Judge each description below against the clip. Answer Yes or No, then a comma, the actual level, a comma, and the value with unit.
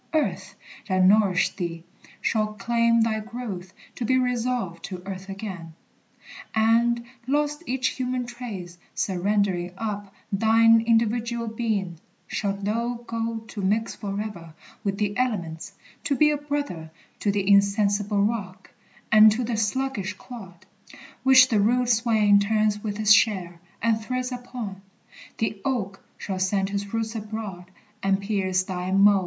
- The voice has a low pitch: No, high, 215 Hz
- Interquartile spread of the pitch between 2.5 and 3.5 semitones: Yes, average, 3.2 semitones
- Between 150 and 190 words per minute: No, average, 140 wpm